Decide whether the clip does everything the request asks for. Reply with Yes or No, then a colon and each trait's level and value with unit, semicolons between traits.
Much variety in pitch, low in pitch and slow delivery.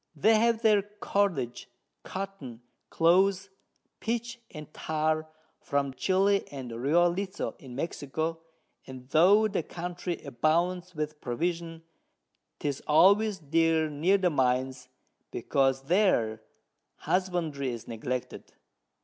No: wide, 5.7 semitones; medium, 165 Hz; slow, 105 wpm